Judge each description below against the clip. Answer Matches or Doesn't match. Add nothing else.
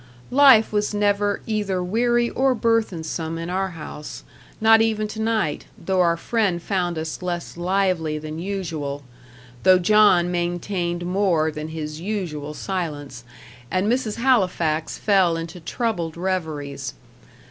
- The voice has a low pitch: Doesn't match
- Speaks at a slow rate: Matches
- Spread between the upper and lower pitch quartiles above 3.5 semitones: Matches